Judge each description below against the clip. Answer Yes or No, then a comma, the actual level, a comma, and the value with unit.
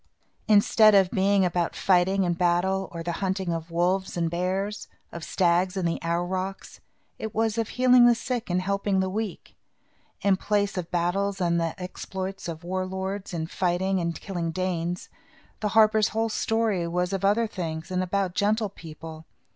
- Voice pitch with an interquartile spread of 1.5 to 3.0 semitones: Yes, narrow, 2.5 semitones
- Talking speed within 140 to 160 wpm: No, average, 170 wpm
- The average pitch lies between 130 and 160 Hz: No, medium, 185 Hz